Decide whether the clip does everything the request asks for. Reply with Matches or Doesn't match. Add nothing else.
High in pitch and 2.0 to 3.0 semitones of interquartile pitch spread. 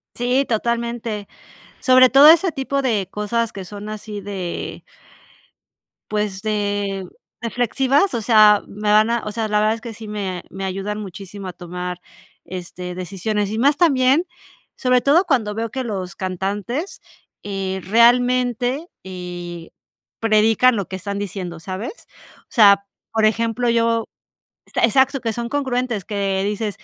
Doesn't match